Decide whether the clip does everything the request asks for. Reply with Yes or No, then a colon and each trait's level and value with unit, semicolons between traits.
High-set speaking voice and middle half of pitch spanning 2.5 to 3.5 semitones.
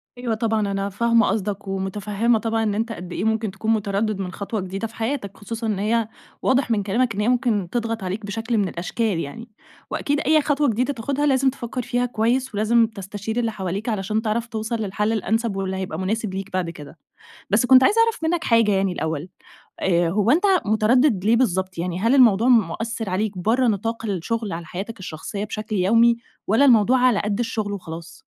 Yes: high, 220 Hz; average, 3.1 semitones